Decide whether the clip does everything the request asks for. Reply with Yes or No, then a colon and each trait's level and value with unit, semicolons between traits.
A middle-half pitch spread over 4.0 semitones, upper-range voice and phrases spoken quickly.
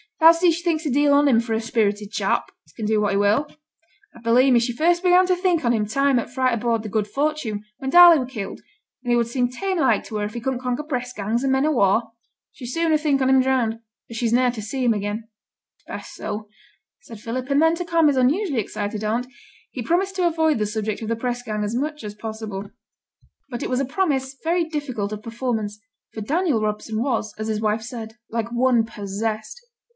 Yes: average, 4.9 semitones; high, 245 Hz; fast, 235 wpm